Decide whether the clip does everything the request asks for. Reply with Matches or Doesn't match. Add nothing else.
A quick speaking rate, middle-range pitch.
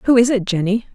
Doesn't match